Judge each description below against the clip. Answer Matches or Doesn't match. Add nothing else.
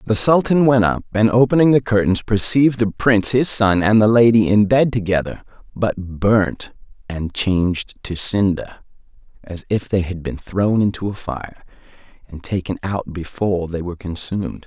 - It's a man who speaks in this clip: Matches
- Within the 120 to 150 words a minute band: Doesn't match